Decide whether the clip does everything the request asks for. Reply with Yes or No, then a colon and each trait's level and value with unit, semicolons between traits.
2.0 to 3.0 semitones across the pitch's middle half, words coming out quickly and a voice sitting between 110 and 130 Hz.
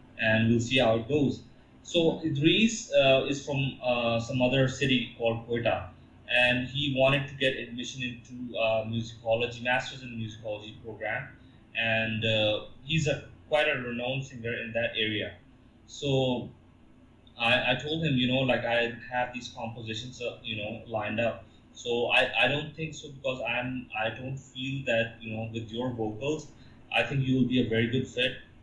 No: narrow, 2.5 semitones; average, 180 wpm; low, 125 Hz